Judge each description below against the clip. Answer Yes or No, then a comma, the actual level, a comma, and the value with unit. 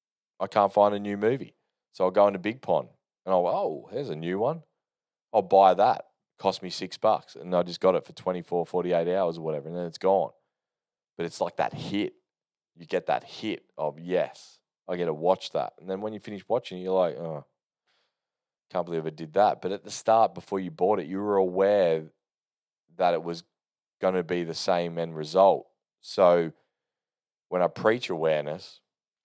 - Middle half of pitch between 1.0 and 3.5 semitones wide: Yes, narrow, 2.4 semitones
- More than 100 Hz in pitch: No, very low, 90 Hz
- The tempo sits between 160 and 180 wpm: No, average, 200 wpm